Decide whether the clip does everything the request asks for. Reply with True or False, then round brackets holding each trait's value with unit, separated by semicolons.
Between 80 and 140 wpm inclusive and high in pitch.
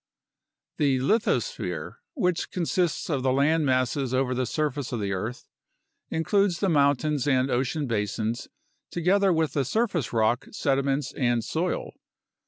False (135 wpm; 140 Hz)